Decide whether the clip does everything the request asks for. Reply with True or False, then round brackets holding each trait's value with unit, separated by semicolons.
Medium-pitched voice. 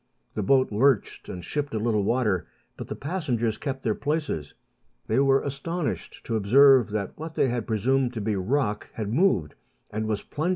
False (120 Hz)